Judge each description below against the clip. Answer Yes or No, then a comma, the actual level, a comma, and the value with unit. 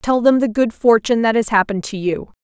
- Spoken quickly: Yes, fast, 245 wpm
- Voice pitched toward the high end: Yes, high, 225 Hz